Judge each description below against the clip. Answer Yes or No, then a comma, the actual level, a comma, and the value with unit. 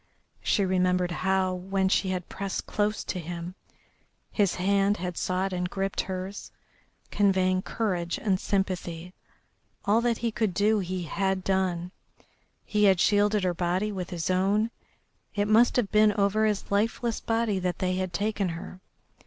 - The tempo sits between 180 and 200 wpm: No, average, 155 wpm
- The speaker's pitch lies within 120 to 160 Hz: No, high, 190 Hz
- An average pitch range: No, narrow, 2.2 semitones